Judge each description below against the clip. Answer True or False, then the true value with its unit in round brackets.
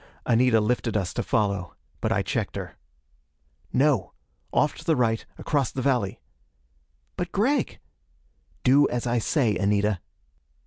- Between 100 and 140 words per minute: True (135 wpm)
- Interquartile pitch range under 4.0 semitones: False (4.8 semitones)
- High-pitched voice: False (120 Hz)